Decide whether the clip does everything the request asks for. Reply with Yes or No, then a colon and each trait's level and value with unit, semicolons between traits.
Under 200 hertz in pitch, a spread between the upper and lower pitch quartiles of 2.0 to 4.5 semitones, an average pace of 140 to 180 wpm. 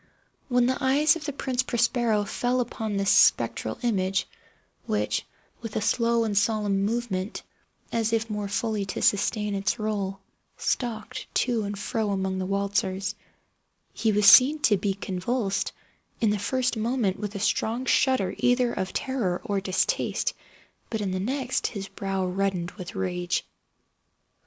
No: high, 210 Hz; average, 3.5 semitones; average, 150 wpm